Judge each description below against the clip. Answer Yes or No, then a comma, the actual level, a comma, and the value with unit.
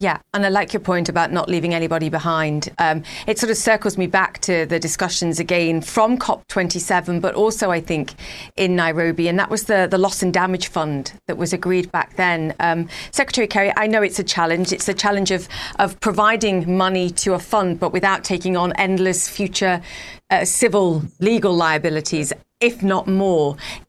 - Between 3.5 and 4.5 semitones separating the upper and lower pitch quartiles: No, average, 2.9 semitones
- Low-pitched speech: No, medium, 185 Hz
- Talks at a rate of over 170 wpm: Yes, average, 190 wpm